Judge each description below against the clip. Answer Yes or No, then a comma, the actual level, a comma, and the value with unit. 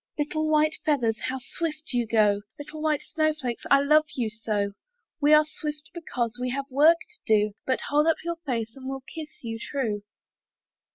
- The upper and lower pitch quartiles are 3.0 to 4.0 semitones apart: No, average, 4.9 semitones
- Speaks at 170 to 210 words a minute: Yes, average, 180 wpm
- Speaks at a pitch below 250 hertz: No, very high, 280 Hz